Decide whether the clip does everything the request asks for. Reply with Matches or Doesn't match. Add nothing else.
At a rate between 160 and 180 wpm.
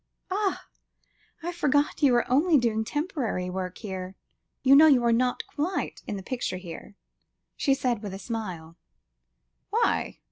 Doesn't match